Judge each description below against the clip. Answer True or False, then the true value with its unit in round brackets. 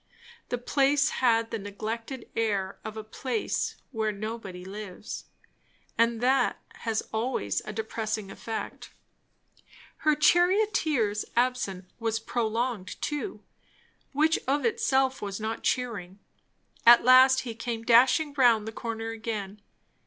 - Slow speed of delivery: True (120 wpm)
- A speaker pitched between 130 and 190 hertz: False (230 Hz)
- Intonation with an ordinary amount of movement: True (3.2 semitones)